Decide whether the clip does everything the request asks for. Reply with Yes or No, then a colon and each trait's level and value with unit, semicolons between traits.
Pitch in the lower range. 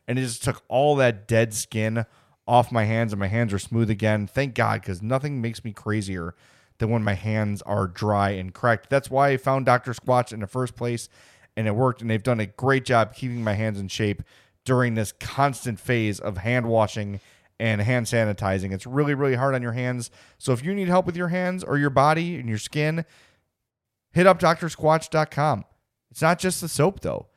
Yes: low, 120 Hz